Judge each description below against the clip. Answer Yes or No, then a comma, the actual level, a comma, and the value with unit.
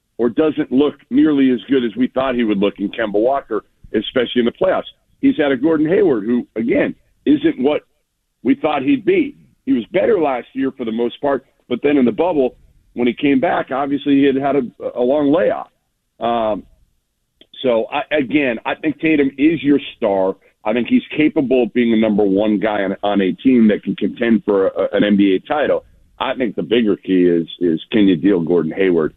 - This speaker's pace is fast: Yes, fast, 210 wpm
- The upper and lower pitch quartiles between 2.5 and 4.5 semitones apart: No, wide, 5.6 semitones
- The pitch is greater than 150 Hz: No, low, 135 Hz